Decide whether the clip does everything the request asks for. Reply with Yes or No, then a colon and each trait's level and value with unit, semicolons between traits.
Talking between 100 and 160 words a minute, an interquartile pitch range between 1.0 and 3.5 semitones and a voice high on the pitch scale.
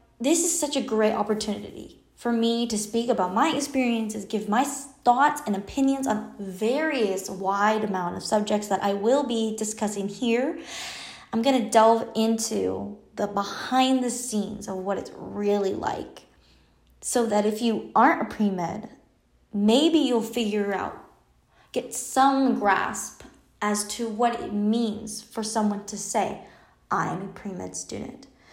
Yes: average, 150 wpm; average, 3.2 semitones; high, 220 Hz